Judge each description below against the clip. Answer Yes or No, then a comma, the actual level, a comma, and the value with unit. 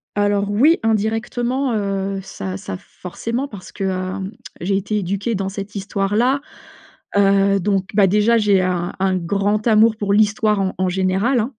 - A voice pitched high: Yes, high, 200 Hz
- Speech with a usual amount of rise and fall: No, narrow, 2.2 semitones